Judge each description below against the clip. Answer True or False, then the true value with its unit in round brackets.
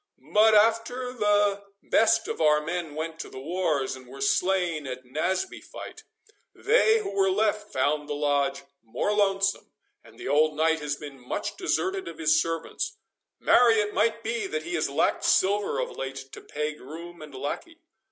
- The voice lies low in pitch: False (175 Hz)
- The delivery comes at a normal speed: True (170 wpm)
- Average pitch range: False (6.5 semitones)